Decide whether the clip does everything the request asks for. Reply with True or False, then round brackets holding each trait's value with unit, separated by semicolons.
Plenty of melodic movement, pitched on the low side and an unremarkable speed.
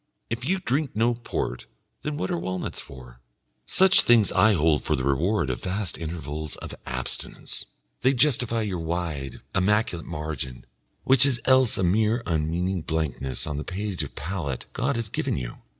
True (7.2 semitones; 90 Hz; 165 wpm)